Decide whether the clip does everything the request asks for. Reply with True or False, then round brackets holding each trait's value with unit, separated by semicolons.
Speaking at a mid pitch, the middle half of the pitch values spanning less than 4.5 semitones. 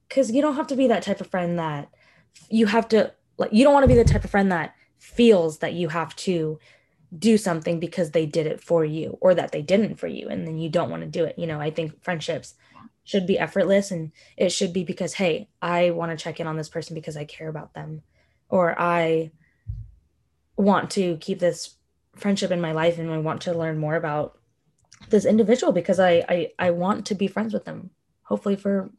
True (170 Hz; 3.4 semitones)